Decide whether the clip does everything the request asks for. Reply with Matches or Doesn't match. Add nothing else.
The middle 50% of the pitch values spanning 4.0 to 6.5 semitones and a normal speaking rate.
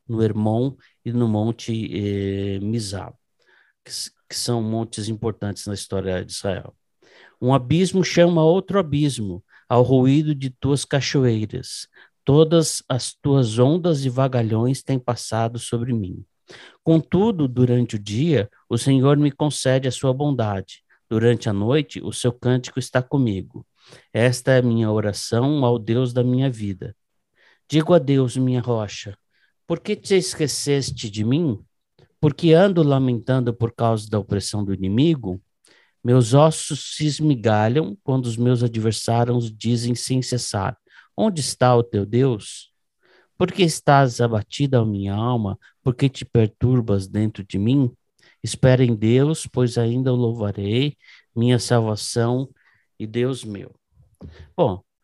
Doesn't match